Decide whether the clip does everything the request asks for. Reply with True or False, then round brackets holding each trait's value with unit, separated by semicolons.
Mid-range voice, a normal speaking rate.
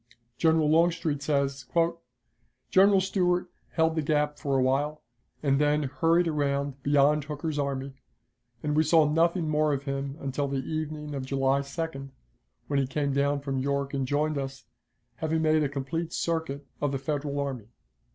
True (145 Hz; 160 wpm)